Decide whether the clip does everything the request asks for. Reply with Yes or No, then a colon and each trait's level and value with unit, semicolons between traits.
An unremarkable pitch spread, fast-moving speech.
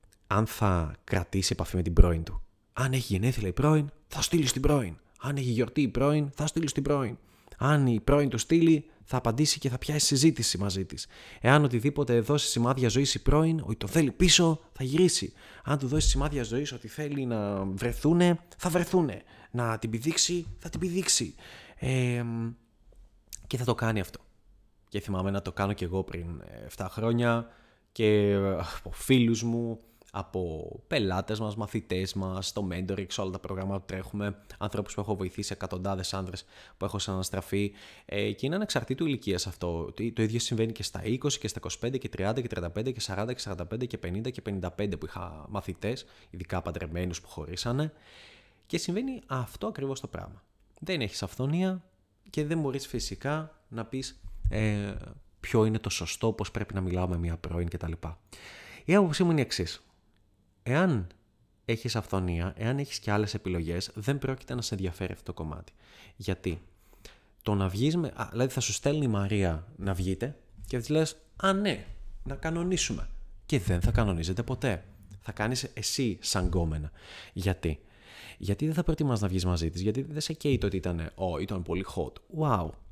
No: wide, 5.7 semitones; fast, 175 wpm